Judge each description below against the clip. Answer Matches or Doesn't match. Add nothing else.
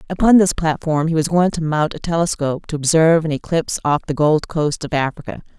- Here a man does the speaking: Doesn't match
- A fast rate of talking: Matches